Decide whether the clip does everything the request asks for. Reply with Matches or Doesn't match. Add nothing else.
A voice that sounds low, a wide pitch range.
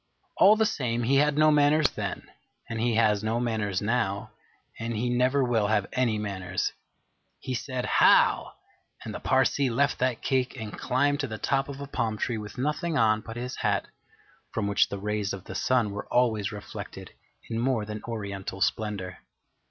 Doesn't match